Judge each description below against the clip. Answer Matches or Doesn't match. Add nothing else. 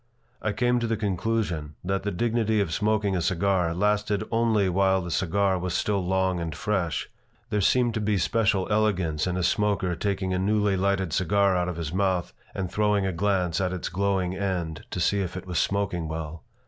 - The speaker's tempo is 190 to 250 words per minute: Matches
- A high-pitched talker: Doesn't match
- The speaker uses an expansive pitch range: Doesn't match